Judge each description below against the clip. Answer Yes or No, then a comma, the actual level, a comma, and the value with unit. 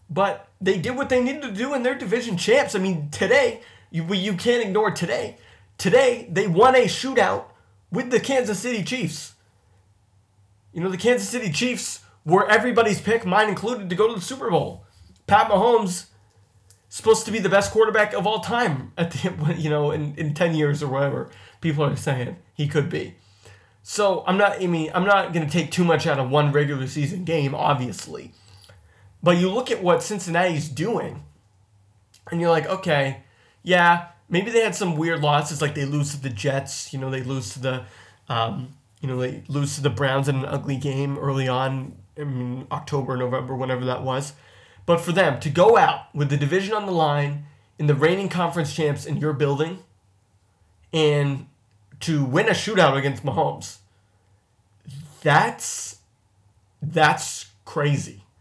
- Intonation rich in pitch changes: Yes, wide, 6.8 semitones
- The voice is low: No, medium, 145 Hz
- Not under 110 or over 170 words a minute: No, average, 180 wpm